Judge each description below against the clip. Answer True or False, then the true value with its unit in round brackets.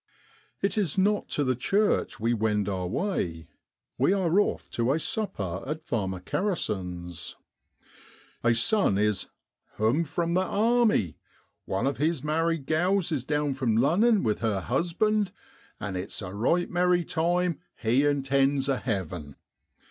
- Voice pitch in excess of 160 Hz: False (140 Hz)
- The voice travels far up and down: True (8.8 semitones)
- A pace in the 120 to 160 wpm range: True (150 wpm)